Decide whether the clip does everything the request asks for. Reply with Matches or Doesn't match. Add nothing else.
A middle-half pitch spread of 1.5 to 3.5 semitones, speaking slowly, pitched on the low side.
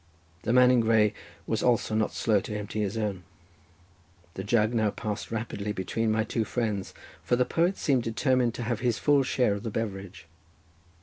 Doesn't match